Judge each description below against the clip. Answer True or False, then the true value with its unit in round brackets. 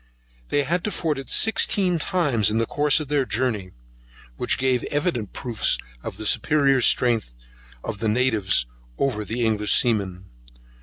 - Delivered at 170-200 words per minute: False (155 wpm)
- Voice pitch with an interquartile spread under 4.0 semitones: False (5.4 semitones)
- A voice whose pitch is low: True (125 Hz)